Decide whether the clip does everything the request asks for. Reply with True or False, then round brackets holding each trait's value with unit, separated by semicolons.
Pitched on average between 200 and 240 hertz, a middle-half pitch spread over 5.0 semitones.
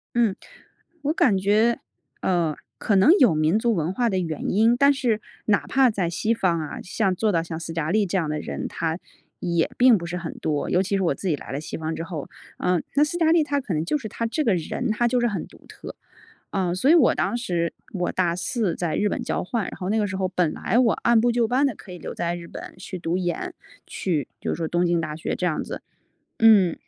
False (190 Hz; 5.4 semitones)